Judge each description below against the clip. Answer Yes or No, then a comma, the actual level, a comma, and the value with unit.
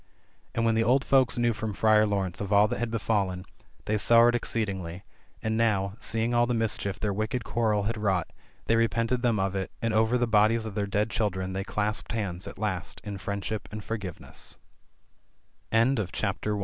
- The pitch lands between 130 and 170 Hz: No, low, 110 Hz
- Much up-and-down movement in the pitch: No, narrow, 2.4 semitones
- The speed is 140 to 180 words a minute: Yes, average, 160 wpm